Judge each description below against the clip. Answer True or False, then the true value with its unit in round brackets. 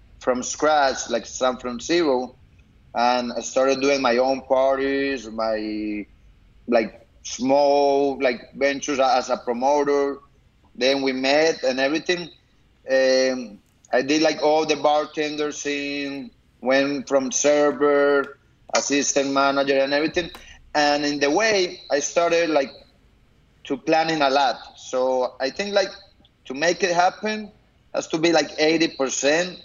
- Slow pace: True (130 wpm)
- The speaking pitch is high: False (140 Hz)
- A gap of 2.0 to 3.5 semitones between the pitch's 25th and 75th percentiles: True (2.6 semitones)